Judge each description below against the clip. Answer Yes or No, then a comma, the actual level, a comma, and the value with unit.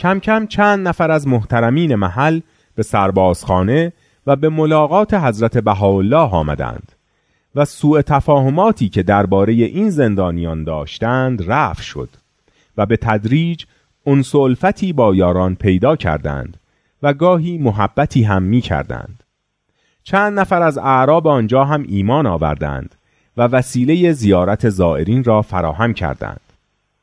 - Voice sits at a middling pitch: No, low, 120 Hz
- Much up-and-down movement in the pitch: Yes, wide, 7.8 semitones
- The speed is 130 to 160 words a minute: No, average, 120 wpm